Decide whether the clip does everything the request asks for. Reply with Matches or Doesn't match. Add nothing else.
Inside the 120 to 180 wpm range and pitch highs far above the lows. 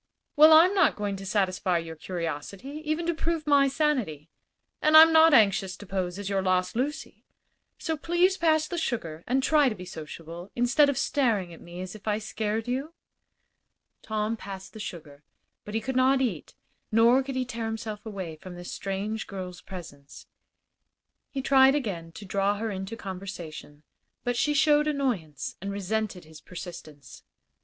Matches